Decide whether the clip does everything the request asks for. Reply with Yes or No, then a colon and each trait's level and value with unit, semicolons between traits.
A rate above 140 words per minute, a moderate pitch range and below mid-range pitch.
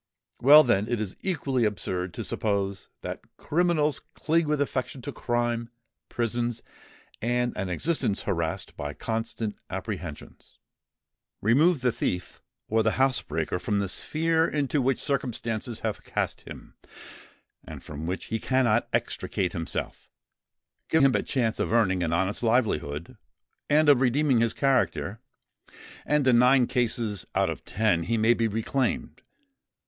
No: slow, 135 wpm; average, 4.7 semitones; low, 120 Hz